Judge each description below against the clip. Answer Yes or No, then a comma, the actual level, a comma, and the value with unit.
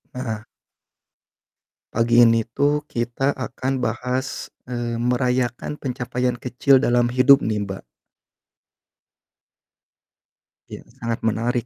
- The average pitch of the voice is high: No, low, 120 Hz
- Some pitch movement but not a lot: No, narrow, 1.6 semitones